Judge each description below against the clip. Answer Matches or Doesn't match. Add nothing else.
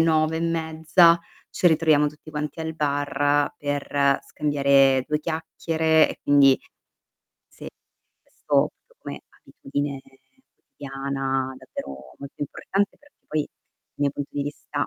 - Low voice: Doesn't match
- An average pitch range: Doesn't match